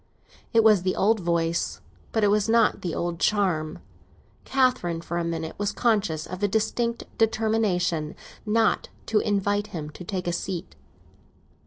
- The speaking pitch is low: No, high, 200 Hz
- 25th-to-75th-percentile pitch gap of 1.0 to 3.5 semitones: No, average, 4.4 semitones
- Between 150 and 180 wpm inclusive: Yes, average, 155 wpm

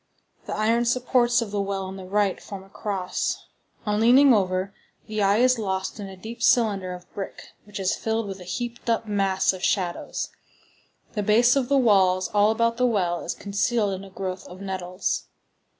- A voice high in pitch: Yes, high, 205 Hz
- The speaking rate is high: No, average, 195 wpm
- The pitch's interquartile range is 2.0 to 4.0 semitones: Yes, average, 3.4 semitones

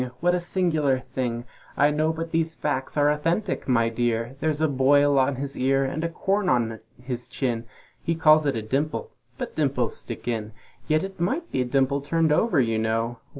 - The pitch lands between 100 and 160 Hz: Yes, medium, 140 Hz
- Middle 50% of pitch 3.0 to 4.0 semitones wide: No, average, 4.6 semitones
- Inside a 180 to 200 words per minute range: Yes, average, 195 wpm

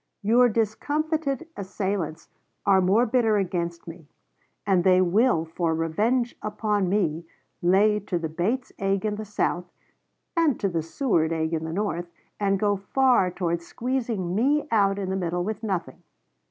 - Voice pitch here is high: Yes, high, 195 Hz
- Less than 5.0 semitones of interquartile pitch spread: Yes, average, 4.2 semitones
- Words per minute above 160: No, average, 155 wpm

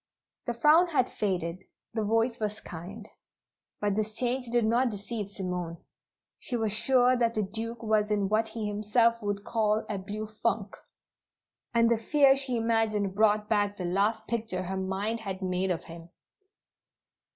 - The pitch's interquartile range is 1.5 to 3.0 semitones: Yes, narrow, 2.6 semitones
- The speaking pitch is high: Yes, high, 215 Hz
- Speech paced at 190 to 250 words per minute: No, average, 165 wpm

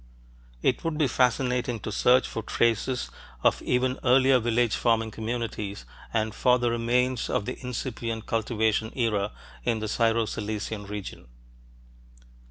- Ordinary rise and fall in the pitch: No, narrow, 2.3 semitones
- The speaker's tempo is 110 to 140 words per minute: Yes, slow, 135 wpm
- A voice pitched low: Yes, low, 115 Hz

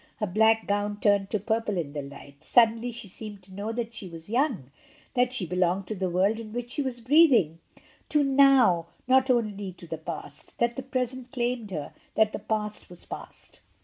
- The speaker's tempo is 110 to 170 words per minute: No, average, 200 wpm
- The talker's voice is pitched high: Yes, high, 215 Hz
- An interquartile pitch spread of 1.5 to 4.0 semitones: No, average, 4.8 semitones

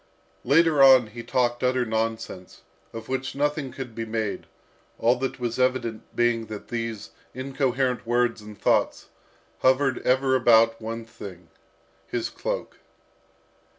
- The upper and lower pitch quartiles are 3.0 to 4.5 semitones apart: No, narrow, 2.5 semitones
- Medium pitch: No, low, 120 Hz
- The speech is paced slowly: Yes, slow, 130 wpm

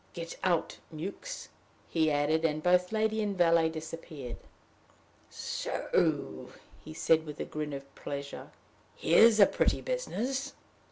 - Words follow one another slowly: Yes, slow, 125 wpm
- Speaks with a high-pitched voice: No, medium, 165 Hz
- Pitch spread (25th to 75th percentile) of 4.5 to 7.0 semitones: Yes, average, 5.0 semitones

